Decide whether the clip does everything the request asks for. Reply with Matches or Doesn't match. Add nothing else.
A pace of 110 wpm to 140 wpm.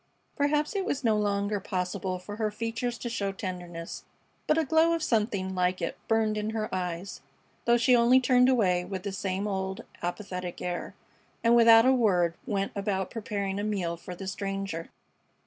Doesn't match